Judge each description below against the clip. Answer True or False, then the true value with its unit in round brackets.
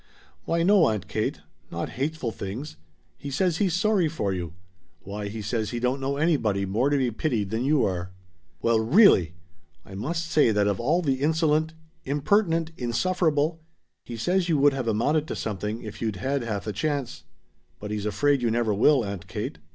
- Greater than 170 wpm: True (190 wpm)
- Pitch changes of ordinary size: False (6.8 semitones)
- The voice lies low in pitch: True (125 Hz)